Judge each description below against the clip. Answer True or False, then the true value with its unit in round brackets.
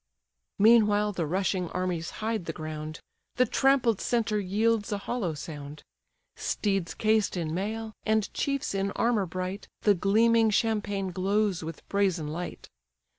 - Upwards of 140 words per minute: False (135 wpm)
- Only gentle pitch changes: False (3.7 semitones)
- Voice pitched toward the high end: True (200 Hz)